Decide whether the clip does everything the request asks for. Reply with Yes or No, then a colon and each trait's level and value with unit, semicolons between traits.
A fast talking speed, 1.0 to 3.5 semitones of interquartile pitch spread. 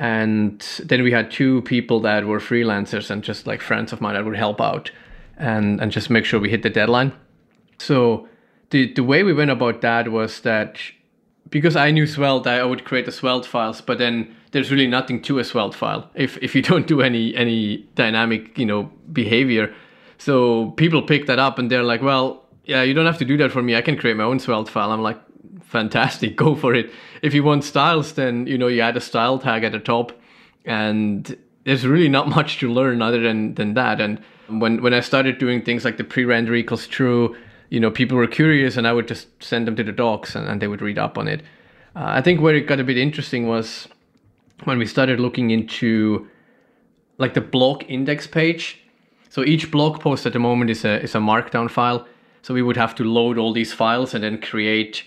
Yes: fast, 220 wpm; average, 3.2 semitones